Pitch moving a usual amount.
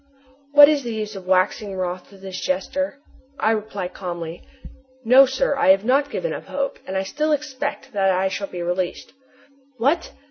No: wide, 6.8 semitones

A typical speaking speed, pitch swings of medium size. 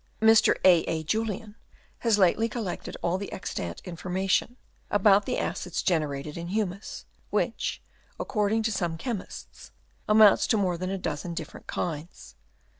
Yes: average, 145 wpm; average, 3.9 semitones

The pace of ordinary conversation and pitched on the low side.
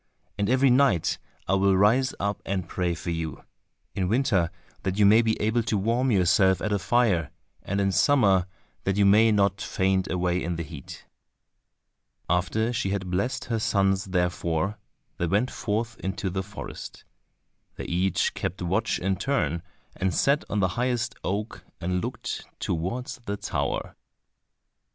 Yes: average, 155 wpm; low, 100 Hz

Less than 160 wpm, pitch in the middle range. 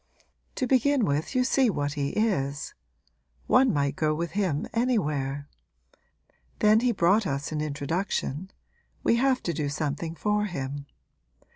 Yes: average, 140 wpm; medium, 170 Hz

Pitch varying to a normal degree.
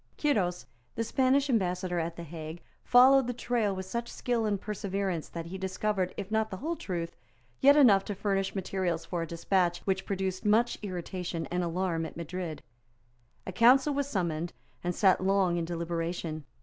Yes: average, 3.9 semitones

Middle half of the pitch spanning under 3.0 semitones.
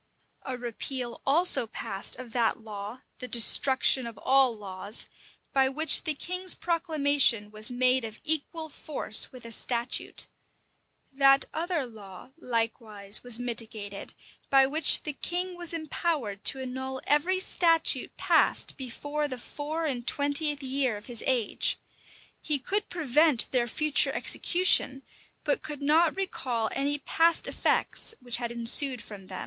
No: average, 4.7 semitones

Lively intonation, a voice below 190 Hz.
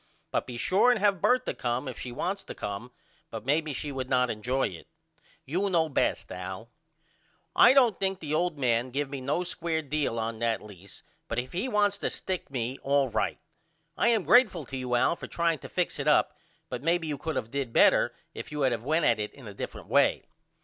Yes: wide, 6.3 semitones; medium, 140 Hz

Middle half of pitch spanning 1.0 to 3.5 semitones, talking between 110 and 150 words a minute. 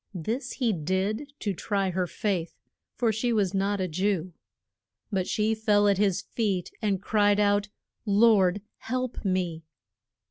Yes: narrow, 2.4 semitones; average, 145 wpm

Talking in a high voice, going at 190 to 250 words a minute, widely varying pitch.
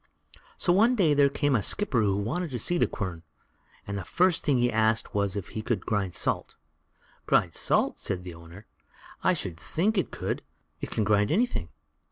No: low, 110 Hz; average, 200 wpm; wide, 8.5 semitones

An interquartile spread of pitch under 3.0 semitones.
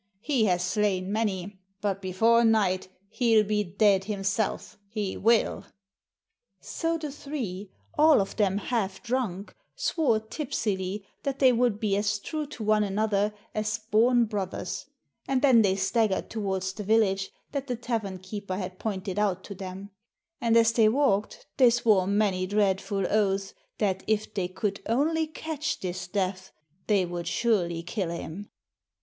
No: average, 3.3 semitones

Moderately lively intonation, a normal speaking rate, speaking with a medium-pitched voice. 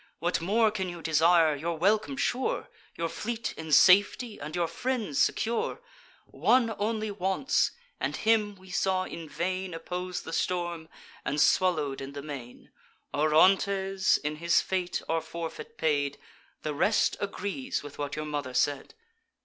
Yes: average, 4.8 semitones; average, 150 wpm; medium, 180 Hz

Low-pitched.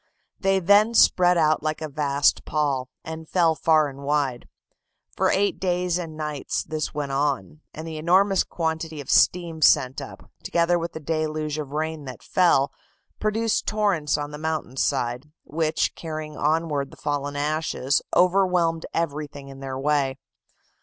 No: medium, 155 Hz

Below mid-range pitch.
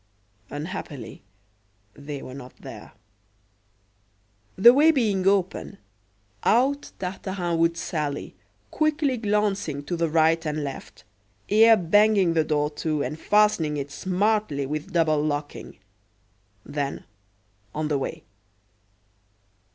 No: medium, 165 Hz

